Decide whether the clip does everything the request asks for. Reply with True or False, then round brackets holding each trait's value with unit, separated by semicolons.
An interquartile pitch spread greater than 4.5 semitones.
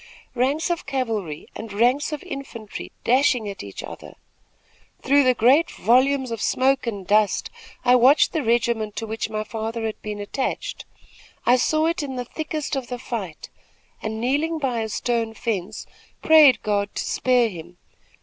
False (4.0 semitones)